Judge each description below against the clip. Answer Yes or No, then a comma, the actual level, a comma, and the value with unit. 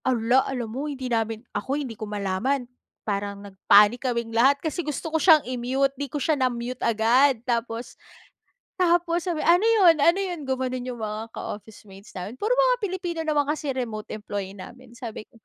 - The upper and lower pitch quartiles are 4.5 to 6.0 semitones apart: Yes, average, 5.1 semitones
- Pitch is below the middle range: No, very high, 255 Hz